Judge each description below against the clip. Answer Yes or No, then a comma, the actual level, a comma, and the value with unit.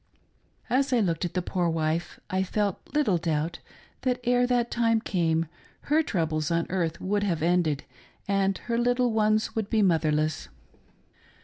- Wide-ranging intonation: Yes, wide, 5.9 semitones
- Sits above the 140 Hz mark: Yes, high, 190 Hz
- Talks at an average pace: Yes, average, 155 wpm